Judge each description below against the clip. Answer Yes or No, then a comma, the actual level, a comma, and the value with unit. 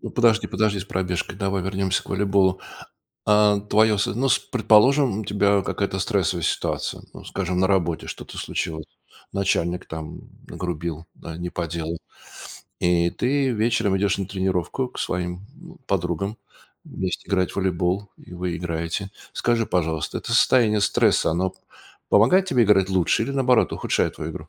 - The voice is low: Yes, very low, 95 Hz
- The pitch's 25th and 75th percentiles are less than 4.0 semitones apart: Yes, average, 3.3 semitones